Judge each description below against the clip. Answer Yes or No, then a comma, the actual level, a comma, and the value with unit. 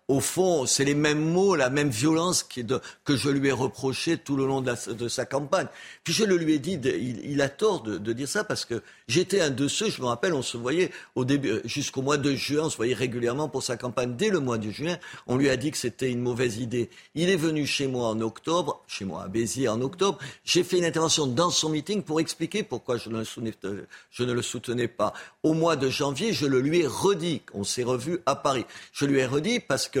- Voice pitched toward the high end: No, medium, 140 Hz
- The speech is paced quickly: Yes, fast, 240 wpm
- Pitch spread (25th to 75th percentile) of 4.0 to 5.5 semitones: Yes, average, 4.8 semitones